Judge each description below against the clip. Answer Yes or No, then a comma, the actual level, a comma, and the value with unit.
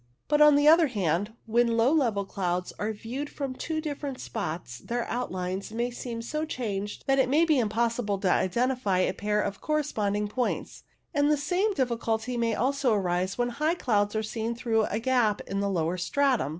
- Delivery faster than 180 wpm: Yes, average, 190 wpm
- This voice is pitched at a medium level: No, high, 235 Hz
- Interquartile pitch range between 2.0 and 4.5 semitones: No, average, 5.0 semitones